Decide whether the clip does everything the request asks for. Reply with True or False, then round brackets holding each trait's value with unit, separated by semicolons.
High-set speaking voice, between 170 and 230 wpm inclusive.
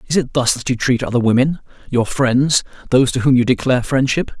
False (125 Hz; 205 wpm)